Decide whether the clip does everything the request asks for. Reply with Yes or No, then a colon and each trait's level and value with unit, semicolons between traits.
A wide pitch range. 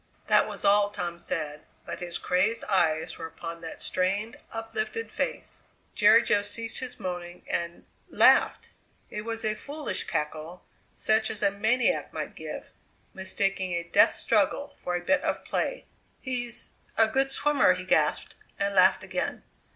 No: average, 4.7 semitones